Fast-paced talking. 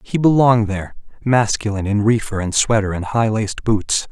No: average, 175 wpm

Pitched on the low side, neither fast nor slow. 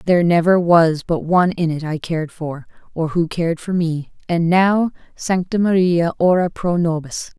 No: medium, 170 Hz; average, 160 wpm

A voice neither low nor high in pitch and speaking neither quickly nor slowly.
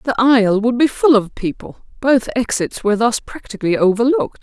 No: high, 240 Hz; average, 175 wpm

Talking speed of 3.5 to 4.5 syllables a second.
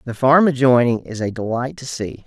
No: 5.1 syllables/s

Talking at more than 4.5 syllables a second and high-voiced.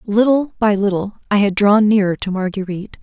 Yes: 5.6 syllables/s; high, 205 Hz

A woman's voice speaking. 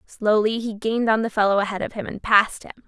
Yes: female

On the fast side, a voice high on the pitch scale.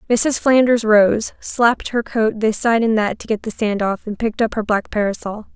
Yes: fast, 225 wpm; high, 220 Hz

